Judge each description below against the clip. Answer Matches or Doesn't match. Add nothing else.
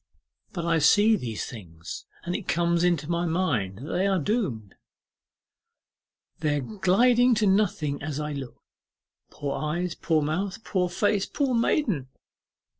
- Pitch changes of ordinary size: Doesn't match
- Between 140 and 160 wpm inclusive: Matches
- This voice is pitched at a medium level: Matches